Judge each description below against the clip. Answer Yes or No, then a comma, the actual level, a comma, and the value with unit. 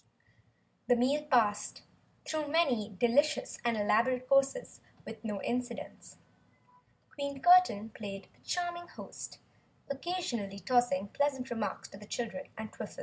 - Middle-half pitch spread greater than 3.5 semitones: Yes, average, 5.1 semitones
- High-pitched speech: Yes, high, 245 Hz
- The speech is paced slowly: Yes, slow, 125 wpm